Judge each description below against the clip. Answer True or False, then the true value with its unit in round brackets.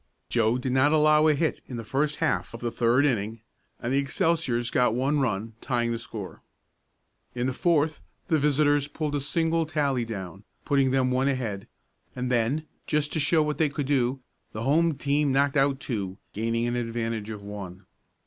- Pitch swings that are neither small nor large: True (4.1 semitones)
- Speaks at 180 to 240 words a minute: True (185 wpm)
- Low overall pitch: True (130 Hz)